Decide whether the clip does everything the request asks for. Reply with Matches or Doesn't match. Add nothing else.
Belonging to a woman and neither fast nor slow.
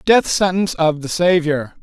Doesn't match